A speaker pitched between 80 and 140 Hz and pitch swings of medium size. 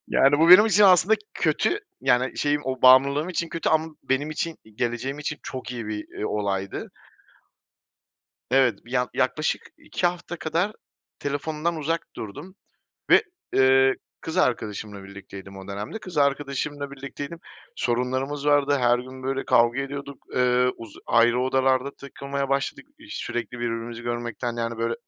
Yes: low, 135 Hz; average, 3.6 semitones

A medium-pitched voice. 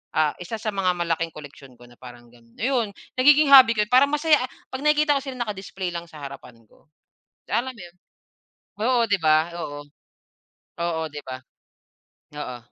Yes: medium, 175 Hz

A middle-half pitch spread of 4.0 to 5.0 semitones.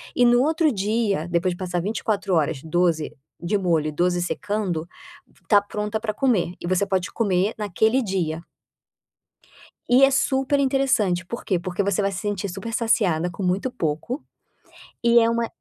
Yes: average, 4.6 semitones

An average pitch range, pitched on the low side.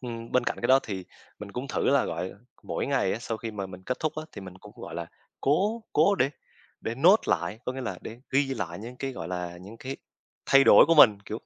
No: wide, 6.0 semitones; low, 115 Hz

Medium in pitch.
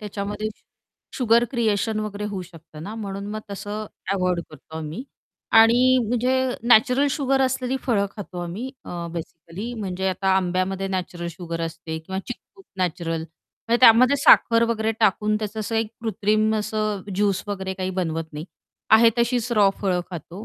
No: high, 205 Hz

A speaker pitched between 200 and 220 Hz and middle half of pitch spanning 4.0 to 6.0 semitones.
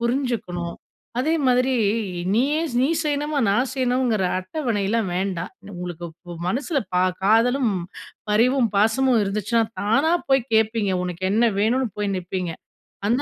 No: high, 230 Hz; average, 4.8 semitones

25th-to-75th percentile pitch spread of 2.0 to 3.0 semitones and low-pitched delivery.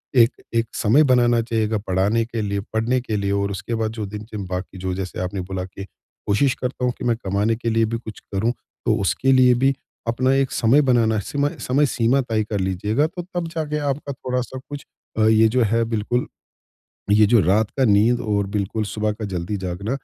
No: average, 3.6 semitones; low, 110 Hz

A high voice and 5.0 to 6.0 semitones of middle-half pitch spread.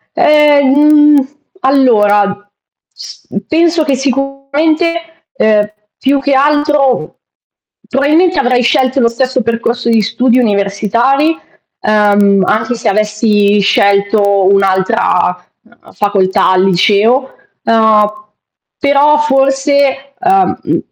Yes: high, 245 Hz; average, 5.3 semitones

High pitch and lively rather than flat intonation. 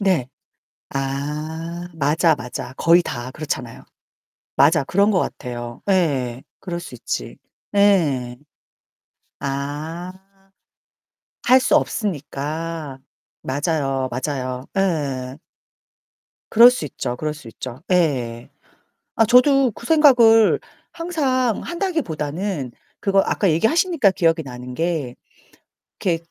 No: medium, 160 Hz; wide, 6.7 semitones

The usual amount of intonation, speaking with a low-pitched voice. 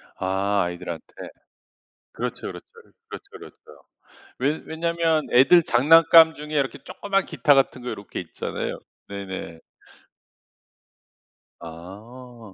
No: wide, 8.3 semitones; low, 125 Hz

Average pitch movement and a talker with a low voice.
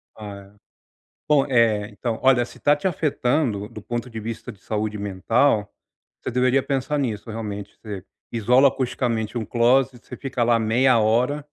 Yes: average, 3.4 semitones; low, 120 Hz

